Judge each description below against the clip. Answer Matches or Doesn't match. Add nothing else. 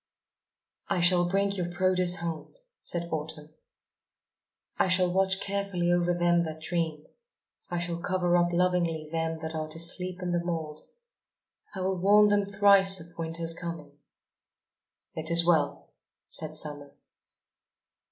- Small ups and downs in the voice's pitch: Matches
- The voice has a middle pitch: Matches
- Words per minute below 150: Matches